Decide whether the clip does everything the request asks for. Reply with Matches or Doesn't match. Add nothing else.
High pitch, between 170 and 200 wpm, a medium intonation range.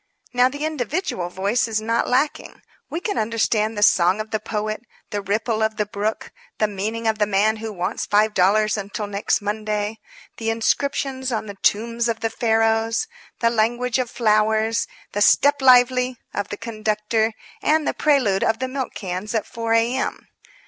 Doesn't match